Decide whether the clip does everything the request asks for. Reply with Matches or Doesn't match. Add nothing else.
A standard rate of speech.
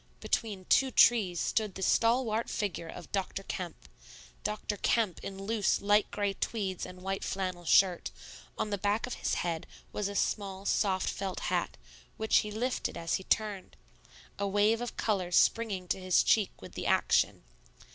Matches